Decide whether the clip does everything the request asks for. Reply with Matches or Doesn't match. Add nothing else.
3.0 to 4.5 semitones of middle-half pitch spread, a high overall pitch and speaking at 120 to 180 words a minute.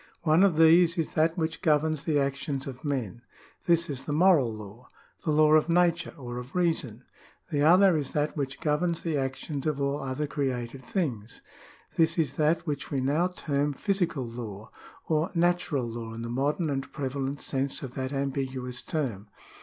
Doesn't match